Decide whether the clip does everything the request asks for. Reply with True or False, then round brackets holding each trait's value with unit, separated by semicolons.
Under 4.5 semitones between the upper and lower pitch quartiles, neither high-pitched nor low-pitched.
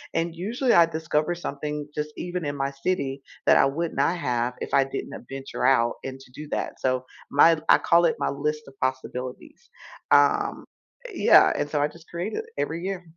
True (3.8 semitones; 150 Hz)